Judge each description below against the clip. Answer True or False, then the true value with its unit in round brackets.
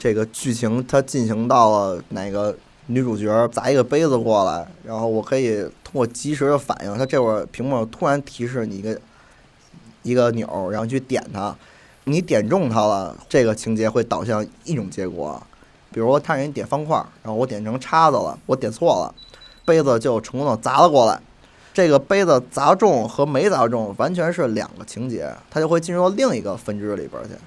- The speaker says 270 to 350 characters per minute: True (290 characters per minute)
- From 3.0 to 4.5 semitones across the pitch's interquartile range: True (4.1 semitones)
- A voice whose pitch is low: True (125 Hz)